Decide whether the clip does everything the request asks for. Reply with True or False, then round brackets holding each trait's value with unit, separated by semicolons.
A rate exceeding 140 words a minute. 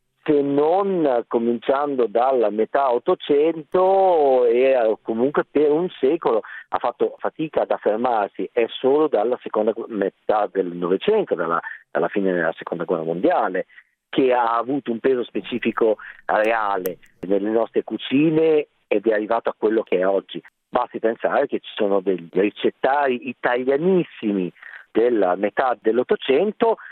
False (130 wpm)